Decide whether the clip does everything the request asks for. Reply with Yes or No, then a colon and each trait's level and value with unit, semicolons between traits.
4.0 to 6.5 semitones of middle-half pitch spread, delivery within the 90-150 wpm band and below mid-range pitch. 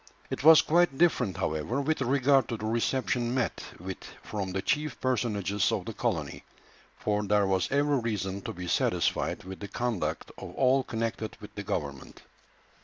No: wide, 5.4 semitones; average, 170 wpm; low, 115 Hz